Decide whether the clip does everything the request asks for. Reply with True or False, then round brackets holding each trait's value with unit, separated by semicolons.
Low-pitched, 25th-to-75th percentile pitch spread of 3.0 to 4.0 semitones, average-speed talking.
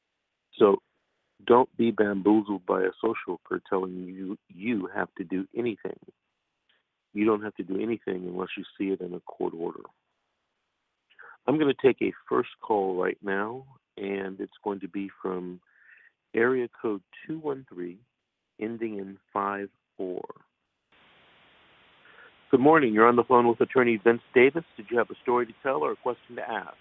True (100 Hz; 3.5 semitones; 165 wpm)